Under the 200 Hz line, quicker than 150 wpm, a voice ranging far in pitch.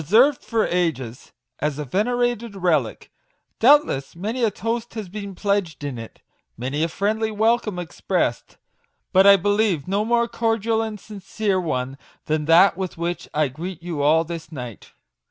Yes: high, 190 Hz; average, 160 wpm; wide, 6.0 semitones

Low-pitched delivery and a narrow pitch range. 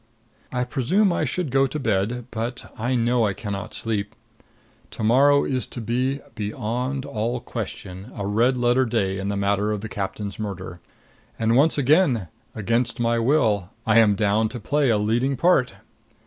No: low, 115 Hz; average, 3.8 semitones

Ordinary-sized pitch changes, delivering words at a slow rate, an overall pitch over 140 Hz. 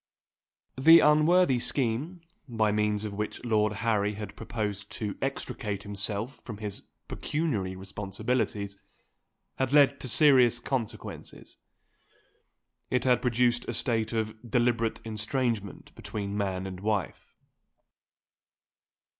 No: average, 3.6 semitones; slow, 110 wpm; low, 110 Hz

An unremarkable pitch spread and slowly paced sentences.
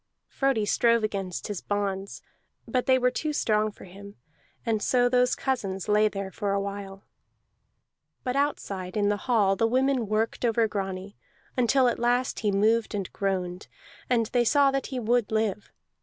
No: average, 3.7 semitones; average, 170 wpm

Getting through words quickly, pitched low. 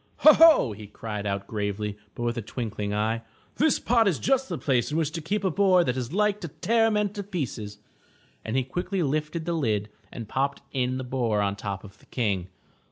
Yes: fast, 220 wpm; low, 130 Hz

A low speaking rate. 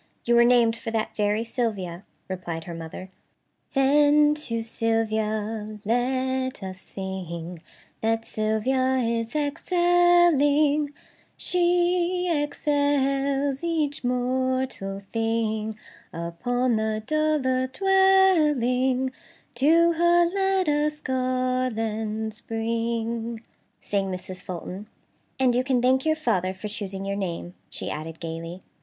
Yes: slow, 110 wpm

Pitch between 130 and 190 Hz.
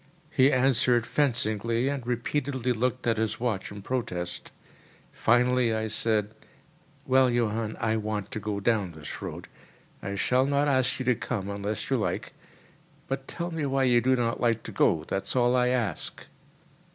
No: low, 120 Hz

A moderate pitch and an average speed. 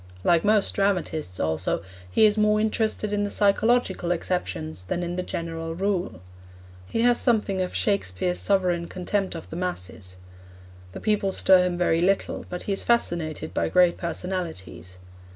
Yes: medium, 180 Hz; average, 155 wpm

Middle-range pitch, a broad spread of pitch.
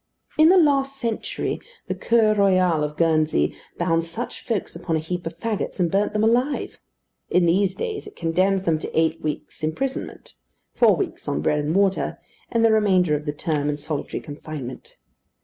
Yes: medium, 180 Hz; wide, 5.8 semitones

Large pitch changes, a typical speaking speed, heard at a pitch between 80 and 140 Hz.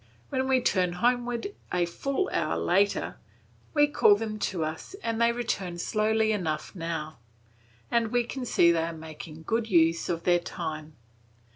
No: wide, 5.9 semitones; average, 160 wpm; high, 190 Hz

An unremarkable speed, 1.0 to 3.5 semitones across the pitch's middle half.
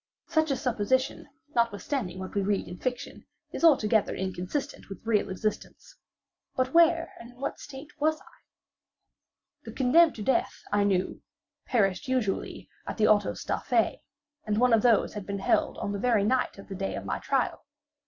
No: average, 175 wpm; average, 4.8 semitones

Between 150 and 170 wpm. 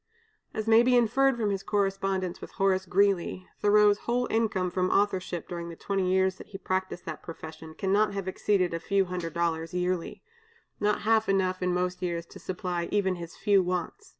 No: average, 185 wpm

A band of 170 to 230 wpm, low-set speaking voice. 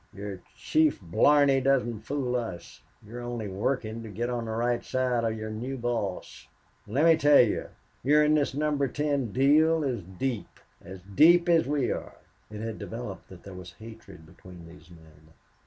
Yes: average, 175 wpm; low, 120 Hz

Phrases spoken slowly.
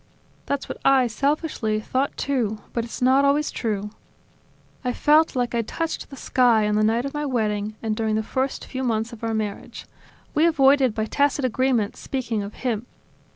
No: average, 190 wpm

